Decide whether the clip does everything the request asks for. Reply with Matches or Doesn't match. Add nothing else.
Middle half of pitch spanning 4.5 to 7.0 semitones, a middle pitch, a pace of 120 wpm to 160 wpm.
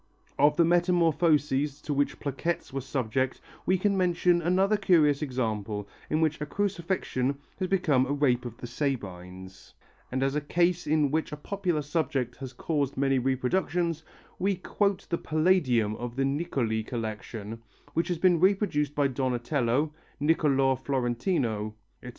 Matches